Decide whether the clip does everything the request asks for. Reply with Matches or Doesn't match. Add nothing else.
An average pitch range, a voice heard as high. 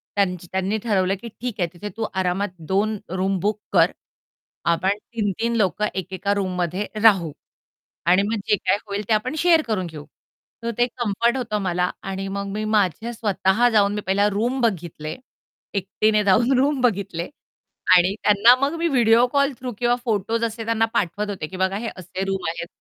Matches